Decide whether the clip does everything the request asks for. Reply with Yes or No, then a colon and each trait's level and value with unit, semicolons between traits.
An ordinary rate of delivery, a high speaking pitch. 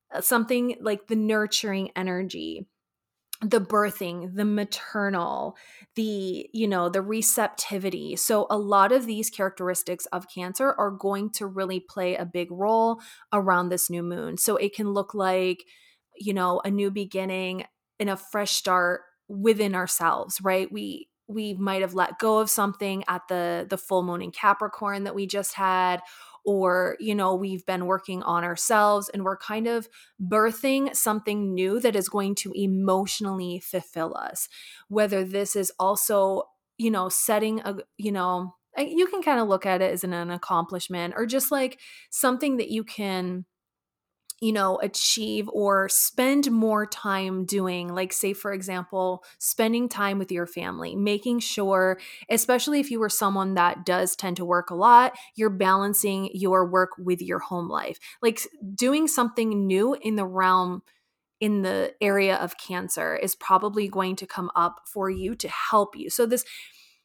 Yes: average, 165 wpm; high, 195 Hz